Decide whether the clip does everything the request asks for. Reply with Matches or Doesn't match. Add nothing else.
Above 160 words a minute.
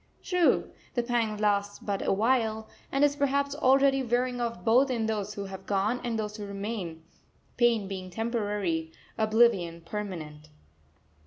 Doesn't match